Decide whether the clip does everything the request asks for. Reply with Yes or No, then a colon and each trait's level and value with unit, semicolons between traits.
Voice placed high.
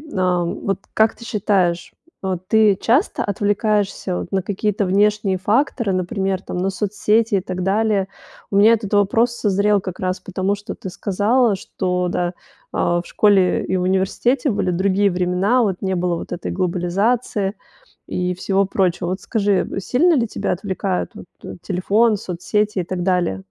Yes: high, 195 Hz